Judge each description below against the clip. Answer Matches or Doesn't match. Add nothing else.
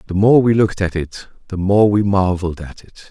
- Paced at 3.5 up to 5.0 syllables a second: Doesn't match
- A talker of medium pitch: Doesn't match